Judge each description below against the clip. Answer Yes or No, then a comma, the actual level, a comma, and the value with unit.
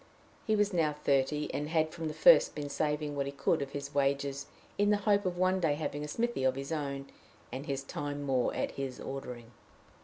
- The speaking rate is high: Yes, fast, 215 wpm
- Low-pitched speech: No, medium, 145 Hz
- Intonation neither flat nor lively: Yes, average, 3.0 semitones